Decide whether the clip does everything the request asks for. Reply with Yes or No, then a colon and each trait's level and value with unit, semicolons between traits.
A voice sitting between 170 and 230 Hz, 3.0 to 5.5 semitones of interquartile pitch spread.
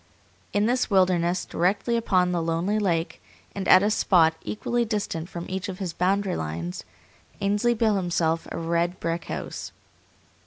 Yes: medium, 185 Hz; average, 3.5 semitones